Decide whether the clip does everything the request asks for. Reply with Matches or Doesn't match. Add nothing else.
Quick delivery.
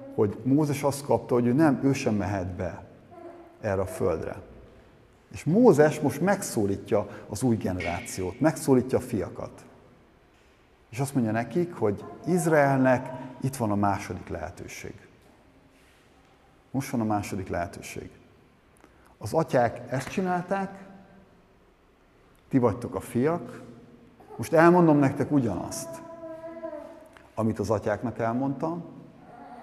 Doesn't match